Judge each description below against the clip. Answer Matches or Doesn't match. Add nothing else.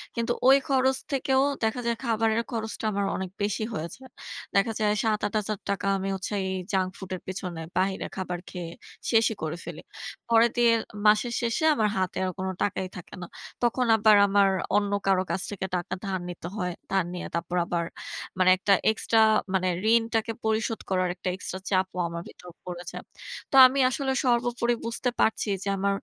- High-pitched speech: Matches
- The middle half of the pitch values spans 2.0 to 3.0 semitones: Doesn't match